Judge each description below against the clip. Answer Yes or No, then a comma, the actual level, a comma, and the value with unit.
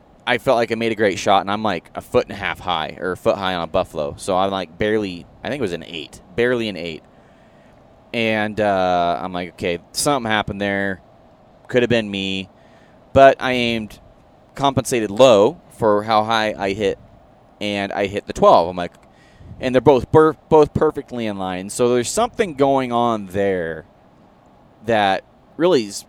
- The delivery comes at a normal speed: Yes, average, 190 wpm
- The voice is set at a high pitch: No, low, 105 Hz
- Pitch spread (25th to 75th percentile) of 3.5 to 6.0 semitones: Yes, average, 4.4 semitones